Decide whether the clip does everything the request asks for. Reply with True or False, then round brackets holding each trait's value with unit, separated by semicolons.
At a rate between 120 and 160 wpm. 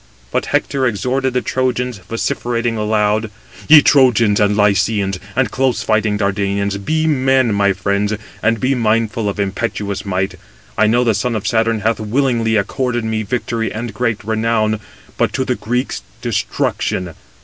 True (150 wpm)